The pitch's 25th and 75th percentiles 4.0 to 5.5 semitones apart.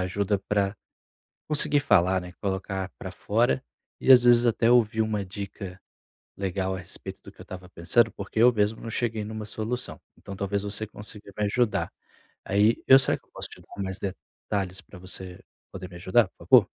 No: average, 2.8 semitones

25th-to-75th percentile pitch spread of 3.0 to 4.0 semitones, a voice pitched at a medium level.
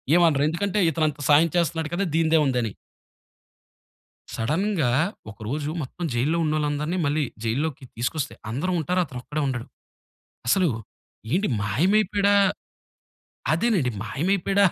No: average, 4.8 semitones; medium, 155 Hz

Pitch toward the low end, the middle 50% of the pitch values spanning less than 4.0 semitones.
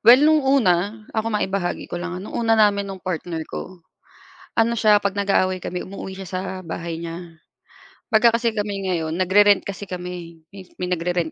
No: high, 190 Hz; average, 3.0 semitones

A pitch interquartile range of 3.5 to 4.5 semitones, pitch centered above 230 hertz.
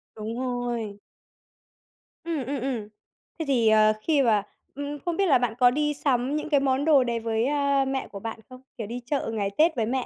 Yes: average, 3.9 semitones; very high, 255 Hz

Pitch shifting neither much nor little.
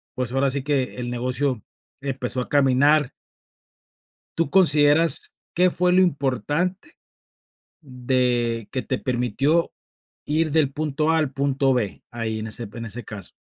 Yes: average, 3.6 semitones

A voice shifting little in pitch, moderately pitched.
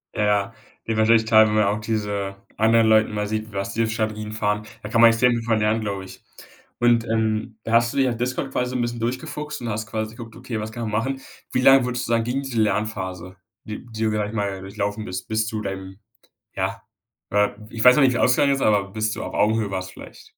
No: narrow, 2.0 semitones; low, 110 Hz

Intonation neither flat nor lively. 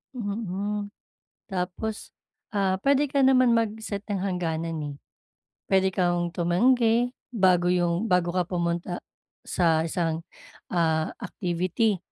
Yes: average, 4.1 semitones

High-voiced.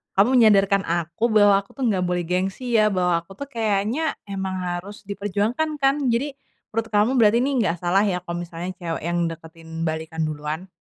Yes: high, 195 Hz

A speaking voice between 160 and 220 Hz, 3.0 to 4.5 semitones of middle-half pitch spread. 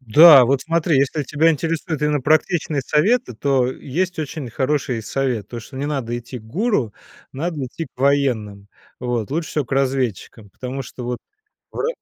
No: low, 135 Hz; average, 4.1 semitones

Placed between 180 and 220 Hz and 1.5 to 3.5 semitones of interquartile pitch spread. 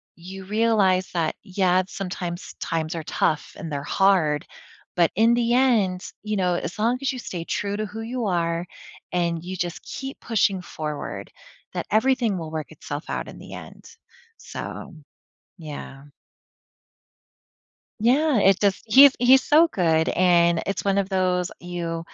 No: medium, 185 Hz; average, 4.2 semitones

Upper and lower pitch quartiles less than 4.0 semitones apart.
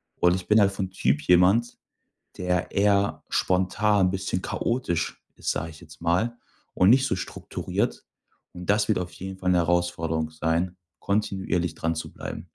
Yes: average, 2.7 semitones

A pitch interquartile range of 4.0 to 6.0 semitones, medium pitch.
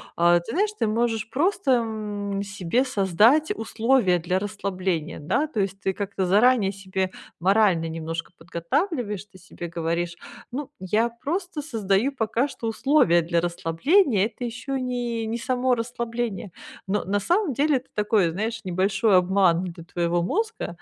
No: average, 5.2 semitones; high, 210 Hz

